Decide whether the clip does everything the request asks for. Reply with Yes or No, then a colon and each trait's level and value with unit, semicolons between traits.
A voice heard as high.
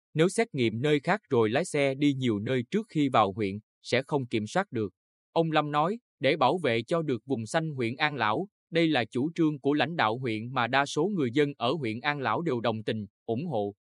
No: low, 130 Hz